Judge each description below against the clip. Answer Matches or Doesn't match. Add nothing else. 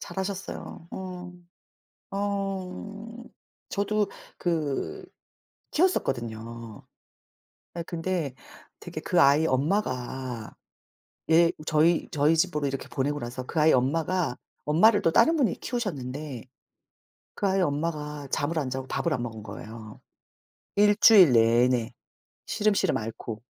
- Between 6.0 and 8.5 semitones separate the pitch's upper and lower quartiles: Matches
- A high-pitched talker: Doesn't match